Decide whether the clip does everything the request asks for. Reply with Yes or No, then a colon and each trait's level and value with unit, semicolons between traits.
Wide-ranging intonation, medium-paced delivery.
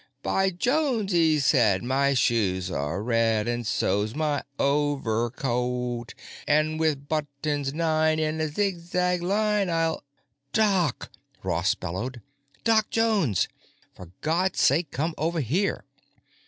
No: wide, 6.1 semitones; slow, 115 wpm